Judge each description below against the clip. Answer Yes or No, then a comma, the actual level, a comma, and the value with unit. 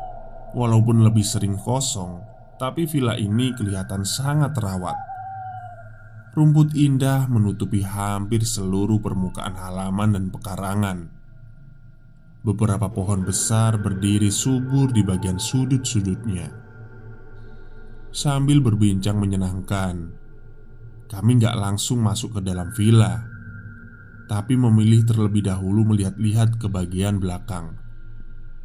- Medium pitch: No, low, 110 Hz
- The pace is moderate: Yes, average, 95 wpm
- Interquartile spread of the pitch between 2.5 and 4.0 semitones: Yes, average, 3.1 semitones